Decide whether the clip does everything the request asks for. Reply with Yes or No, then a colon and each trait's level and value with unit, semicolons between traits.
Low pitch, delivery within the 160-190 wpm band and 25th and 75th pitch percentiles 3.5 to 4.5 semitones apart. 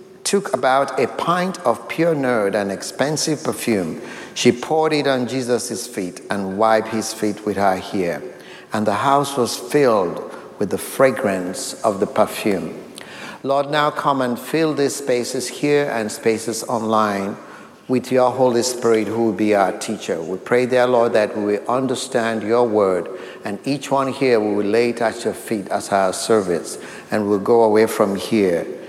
Yes: low, 120 Hz; average, 170 wpm; average, 3.9 semitones